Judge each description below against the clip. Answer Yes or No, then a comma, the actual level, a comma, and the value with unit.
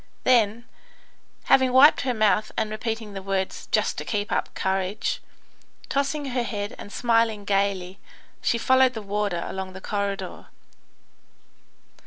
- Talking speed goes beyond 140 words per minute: No, slow, 135 wpm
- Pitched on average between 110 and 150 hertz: No, high, 210 Hz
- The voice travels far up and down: No, average, 3.2 semitones